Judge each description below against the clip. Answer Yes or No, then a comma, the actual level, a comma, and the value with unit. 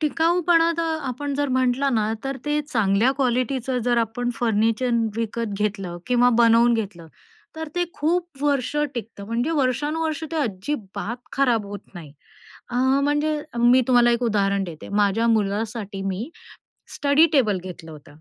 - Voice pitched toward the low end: No, high, 240 Hz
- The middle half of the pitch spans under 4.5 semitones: No, average, 5.3 semitones